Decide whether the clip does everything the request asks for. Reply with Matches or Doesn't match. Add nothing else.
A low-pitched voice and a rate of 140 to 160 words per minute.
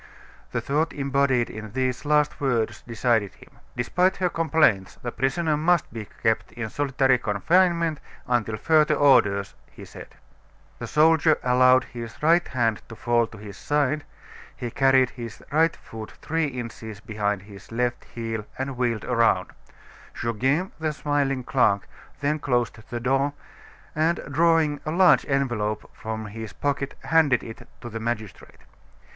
Matches